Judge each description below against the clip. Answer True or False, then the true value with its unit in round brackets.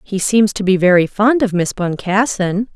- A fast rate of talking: False (195 wpm)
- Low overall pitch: False (200 Hz)